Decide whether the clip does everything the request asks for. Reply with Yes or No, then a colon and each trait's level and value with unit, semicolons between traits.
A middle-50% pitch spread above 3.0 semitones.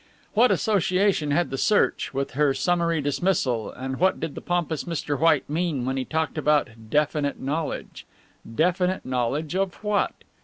Yes: average, 4.4 semitones